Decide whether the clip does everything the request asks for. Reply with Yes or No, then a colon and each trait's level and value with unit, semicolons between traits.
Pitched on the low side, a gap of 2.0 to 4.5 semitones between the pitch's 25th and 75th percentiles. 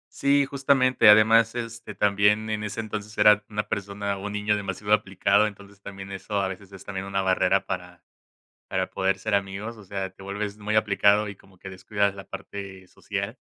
No: low, 100 Hz; narrow, 1.6 semitones